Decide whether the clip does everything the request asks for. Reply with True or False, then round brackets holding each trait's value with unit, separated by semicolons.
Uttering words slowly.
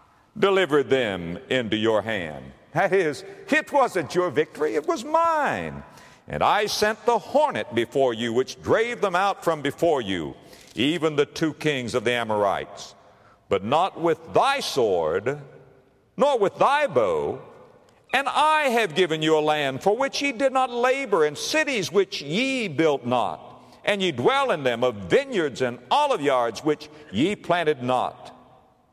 False (160 wpm)